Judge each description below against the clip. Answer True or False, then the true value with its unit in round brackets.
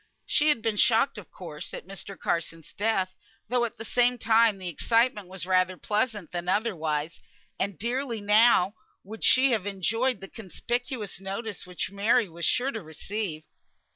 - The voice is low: False (205 Hz)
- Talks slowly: False (165 wpm)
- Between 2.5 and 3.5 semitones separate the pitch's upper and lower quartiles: False (4.0 semitones)